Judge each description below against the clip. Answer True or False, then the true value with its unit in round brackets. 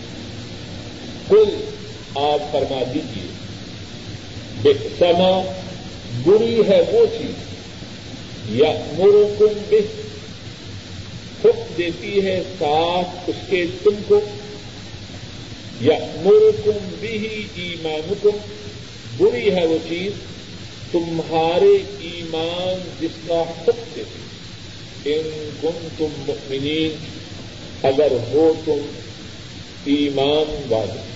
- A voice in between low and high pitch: True (160 Hz)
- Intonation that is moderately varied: False (7.3 semitones)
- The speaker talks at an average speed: False (85 wpm)